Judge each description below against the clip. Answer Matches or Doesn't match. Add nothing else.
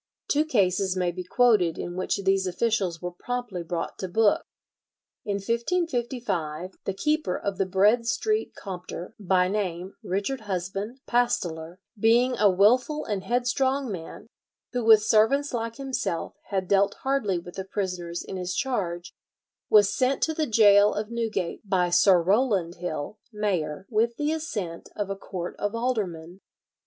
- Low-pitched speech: Doesn't match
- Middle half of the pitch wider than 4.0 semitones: Matches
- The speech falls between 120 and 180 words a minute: Matches